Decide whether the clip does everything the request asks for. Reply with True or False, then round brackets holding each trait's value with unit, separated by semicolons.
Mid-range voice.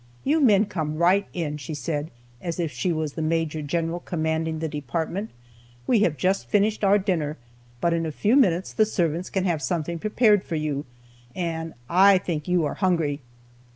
True (170 Hz)